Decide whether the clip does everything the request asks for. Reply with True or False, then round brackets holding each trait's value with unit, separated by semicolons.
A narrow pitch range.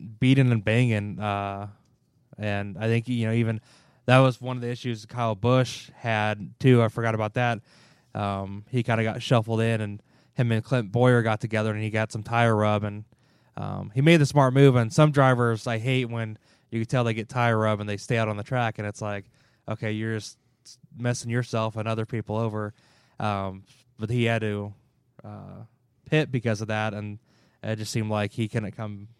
True (2.3 semitones)